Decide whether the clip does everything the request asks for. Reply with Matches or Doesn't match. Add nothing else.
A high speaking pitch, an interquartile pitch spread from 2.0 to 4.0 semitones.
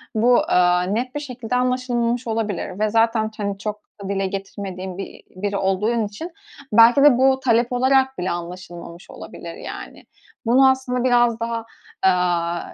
Doesn't match